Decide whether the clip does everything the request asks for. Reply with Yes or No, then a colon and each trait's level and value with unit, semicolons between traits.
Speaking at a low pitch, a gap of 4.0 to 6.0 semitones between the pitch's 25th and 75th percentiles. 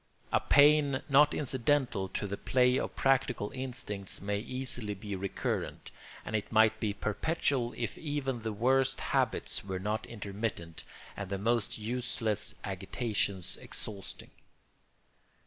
Yes: low, 110 Hz; average, 4.4 semitones